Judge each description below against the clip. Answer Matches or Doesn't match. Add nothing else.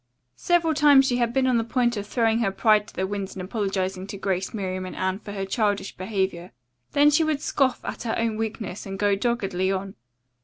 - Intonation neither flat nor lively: Matches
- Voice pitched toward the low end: Doesn't match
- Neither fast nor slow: Doesn't match